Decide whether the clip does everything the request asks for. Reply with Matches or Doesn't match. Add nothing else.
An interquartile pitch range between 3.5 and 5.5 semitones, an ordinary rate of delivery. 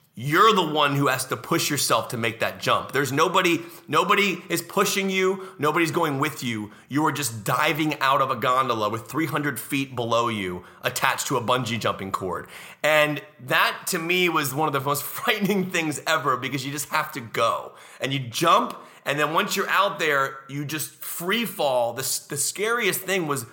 Matches